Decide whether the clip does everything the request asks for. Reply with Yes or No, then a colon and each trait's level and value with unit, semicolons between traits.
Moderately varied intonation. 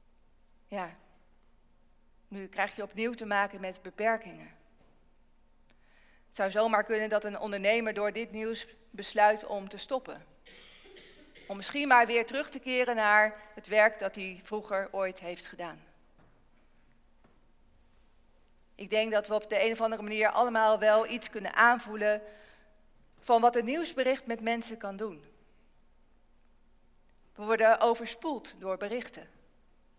No: narrow, 2.2 semitones